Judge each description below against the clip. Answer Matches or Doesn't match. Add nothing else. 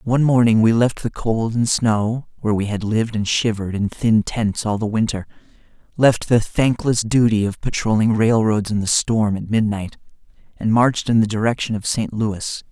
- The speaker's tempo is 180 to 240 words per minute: Matches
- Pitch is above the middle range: Doesn't match